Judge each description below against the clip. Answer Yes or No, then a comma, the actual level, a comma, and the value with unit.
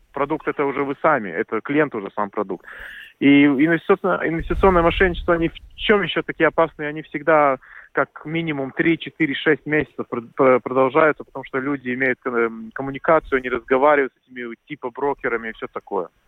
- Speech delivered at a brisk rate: No, average, 150 wpm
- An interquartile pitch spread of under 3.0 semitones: No, average, 3.6 semitones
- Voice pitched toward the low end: No, medium, 145 Hz